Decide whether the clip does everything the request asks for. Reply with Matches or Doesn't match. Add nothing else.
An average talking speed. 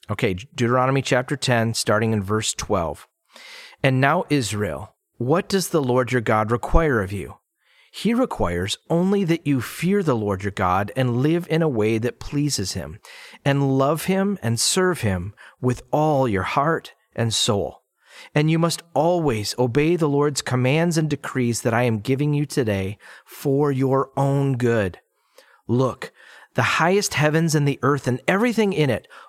Matches